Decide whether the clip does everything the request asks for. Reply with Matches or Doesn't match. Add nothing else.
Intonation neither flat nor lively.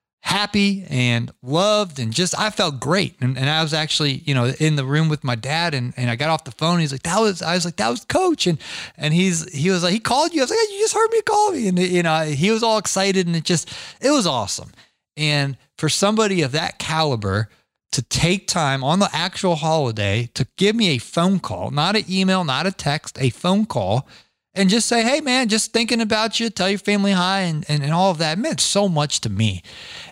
Doesn't match